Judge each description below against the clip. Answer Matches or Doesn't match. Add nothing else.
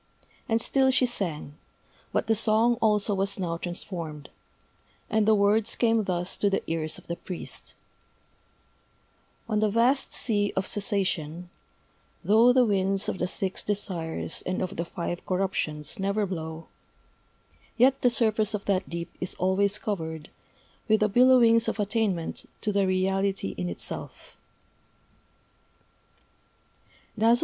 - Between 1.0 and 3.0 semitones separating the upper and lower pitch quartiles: Doesn't match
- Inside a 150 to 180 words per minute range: Doesn't match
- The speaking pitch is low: Doesn't match